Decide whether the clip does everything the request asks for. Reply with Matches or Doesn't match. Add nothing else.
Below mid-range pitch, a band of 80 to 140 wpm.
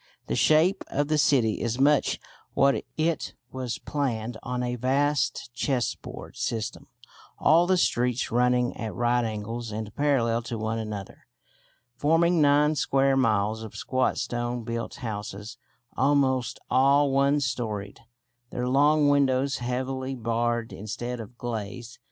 Matches